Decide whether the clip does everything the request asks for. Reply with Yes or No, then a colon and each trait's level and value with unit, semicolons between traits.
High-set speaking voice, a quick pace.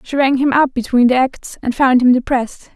Yes: very high, 260 Hz; fast, 240 wpm